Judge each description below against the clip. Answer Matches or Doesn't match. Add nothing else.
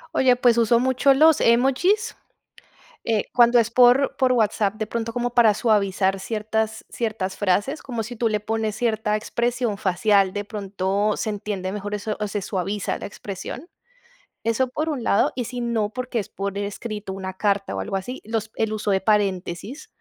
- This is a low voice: Doesn't match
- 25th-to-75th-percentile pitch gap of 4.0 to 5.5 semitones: Doesn't match